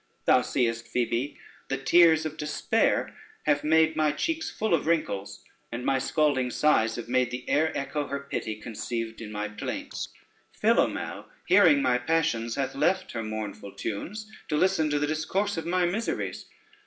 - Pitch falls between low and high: Yes, medium, 145 Hz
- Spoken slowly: No, average, 165 wpm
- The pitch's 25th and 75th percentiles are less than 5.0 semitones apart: No, wide, 5.5 semitones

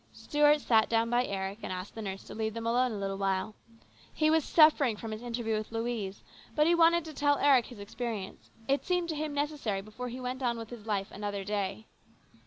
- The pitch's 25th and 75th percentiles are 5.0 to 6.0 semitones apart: Yes, wide, 5.6 semitones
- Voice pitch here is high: Yes, high, 230 Hz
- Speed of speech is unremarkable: No, fast, 220 wpm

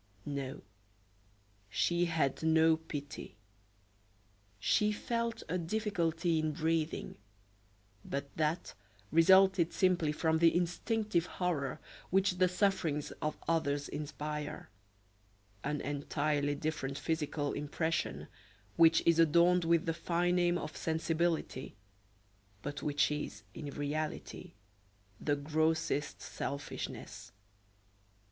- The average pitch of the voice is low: No, medium, 160 Hz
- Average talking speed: No, slow, 100 wpm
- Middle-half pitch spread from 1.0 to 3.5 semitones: Yes, average, 2.8 semitones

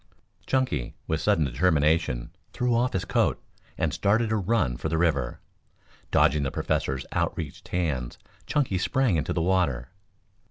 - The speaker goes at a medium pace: Yes, average, 150 wpm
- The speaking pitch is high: No, very low, 80 Hz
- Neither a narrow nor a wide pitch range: No, wide, 6.6 semitones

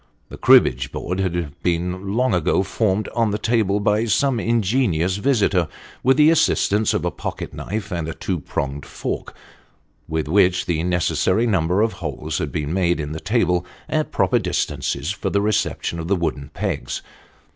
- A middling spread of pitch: Yes, average, 4.3 semitones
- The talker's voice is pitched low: Yes, very low, 95 Hz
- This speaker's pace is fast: No, average, 170 wpm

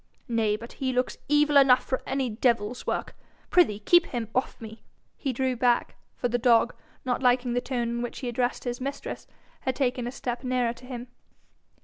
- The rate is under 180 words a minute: No, average, 195 wpm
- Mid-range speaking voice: No, high, 245 Hz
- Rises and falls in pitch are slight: Yes, narrow, 1.6 semitones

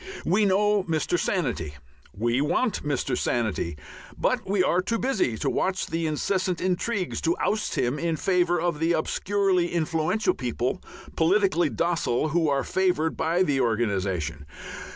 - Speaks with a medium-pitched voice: Yes, medium, 165 Hz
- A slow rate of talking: No, average, 145 wpm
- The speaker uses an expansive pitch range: Yes, wide, 6.1 semitones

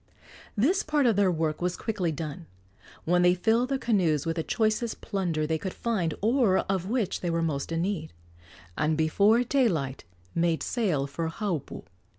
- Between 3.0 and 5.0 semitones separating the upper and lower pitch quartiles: No, wide, 5.5 semitones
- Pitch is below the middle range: No, medium, 180 Hz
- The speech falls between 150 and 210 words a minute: Yes, average, 170 wpm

